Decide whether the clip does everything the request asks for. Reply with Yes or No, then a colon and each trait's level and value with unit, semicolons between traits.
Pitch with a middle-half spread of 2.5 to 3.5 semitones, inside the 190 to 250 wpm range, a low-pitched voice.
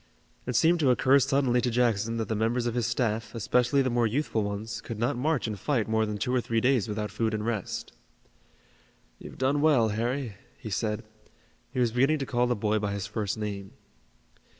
Yes: average, 3.0 semitones; fast, 205 wpm; low, 115 Hz